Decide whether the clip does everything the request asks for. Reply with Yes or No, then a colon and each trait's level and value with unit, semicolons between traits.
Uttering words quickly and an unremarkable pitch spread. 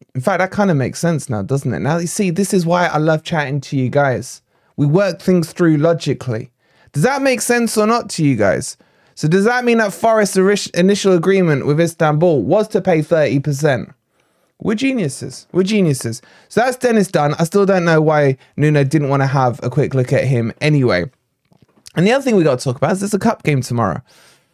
No: fast, 225 wpm; wide, 6.3 semitones